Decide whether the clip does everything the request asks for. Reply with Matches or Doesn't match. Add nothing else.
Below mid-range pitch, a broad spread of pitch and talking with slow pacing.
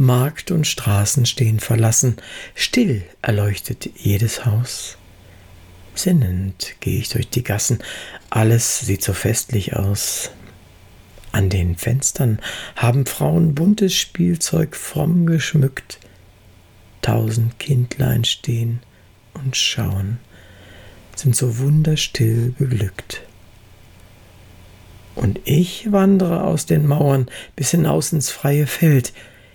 Matches